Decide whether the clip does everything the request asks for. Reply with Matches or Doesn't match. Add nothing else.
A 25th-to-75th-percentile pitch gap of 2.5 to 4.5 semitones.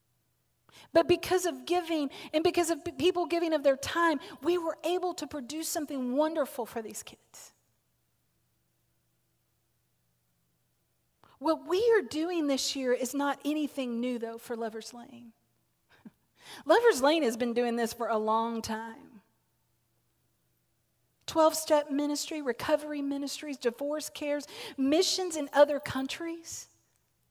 Doesn't match